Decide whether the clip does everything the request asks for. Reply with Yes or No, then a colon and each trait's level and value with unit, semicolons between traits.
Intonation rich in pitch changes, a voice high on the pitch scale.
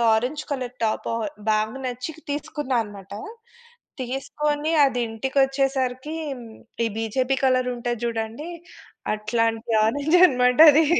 No: average, 3.3 semitones; very high, 250 Hz